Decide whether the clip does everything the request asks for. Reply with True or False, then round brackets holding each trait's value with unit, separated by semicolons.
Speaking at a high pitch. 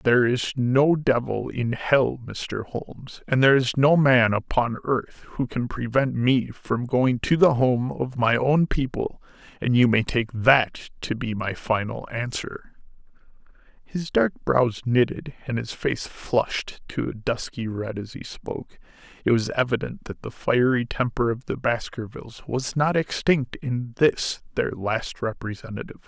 False (125 Hz)